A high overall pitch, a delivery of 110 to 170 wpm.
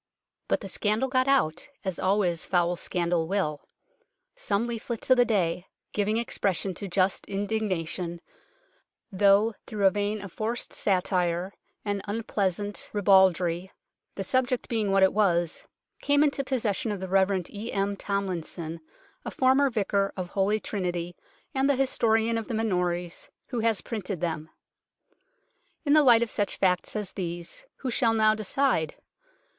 Yes: high, 200 Hz; average, 150 wpm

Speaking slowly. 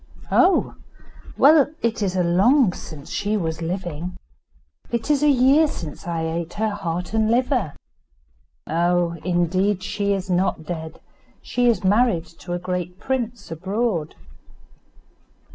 Yes: slow, 130 wpm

